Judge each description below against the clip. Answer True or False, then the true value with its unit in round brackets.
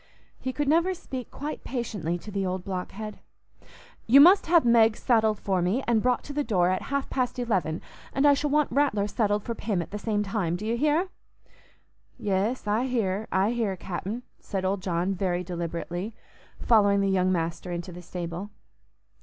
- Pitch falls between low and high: False (210 Hz)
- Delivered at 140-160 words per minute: False (185 wpm)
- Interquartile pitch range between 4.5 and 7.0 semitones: True (5.1 semitones)